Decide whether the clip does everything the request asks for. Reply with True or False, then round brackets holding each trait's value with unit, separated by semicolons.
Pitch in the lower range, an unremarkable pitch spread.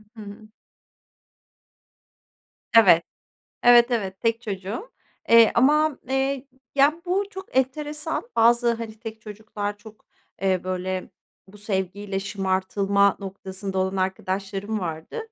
False (210 Hz; 3.9 semitones)